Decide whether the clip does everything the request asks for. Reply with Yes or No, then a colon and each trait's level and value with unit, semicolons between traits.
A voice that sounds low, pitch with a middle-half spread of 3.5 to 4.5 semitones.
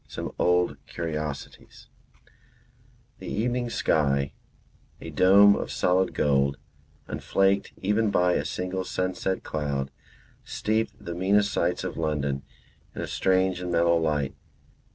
Yes: very low, 90 Hz; average, 4.1 semitones